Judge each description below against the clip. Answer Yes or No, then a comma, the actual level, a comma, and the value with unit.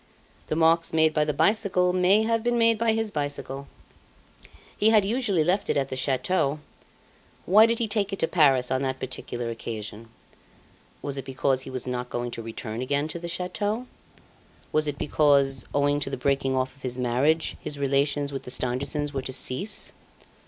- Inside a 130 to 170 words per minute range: No, average, 190 wpm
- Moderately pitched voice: Yes, medium, 145 Hz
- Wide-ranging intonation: Yes, wide, 5.7 semitones